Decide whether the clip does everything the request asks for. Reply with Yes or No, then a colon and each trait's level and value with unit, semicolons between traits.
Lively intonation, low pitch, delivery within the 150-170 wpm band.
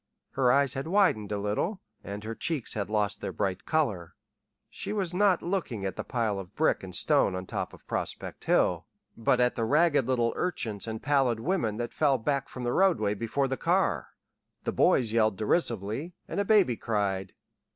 No: wide, 6.0 semitones; low, 120 Hz; average, 190 wpm